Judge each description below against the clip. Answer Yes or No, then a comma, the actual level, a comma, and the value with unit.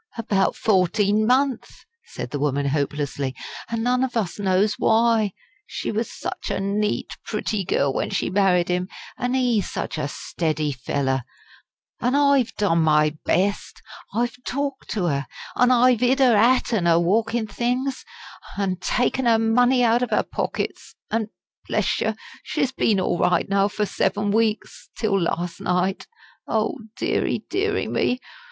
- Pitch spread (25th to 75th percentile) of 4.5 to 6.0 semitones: Yes, wide, 5.4 semitones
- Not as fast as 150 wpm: No, average, 155 wpm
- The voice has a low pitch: No, high, 210 Hz